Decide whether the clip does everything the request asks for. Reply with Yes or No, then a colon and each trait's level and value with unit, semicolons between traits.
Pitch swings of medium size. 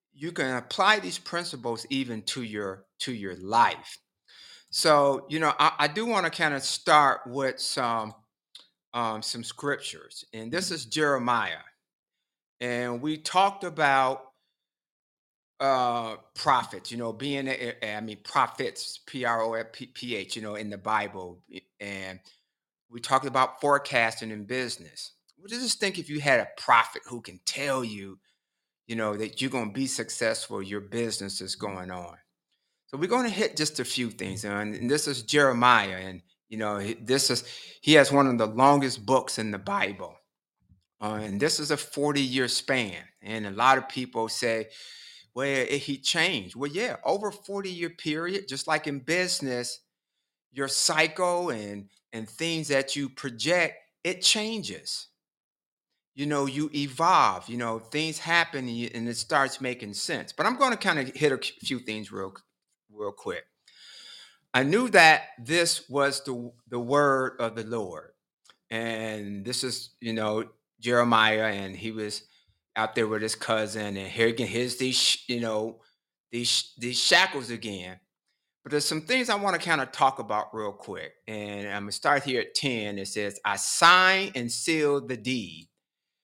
Yes: average, 4.8 semitones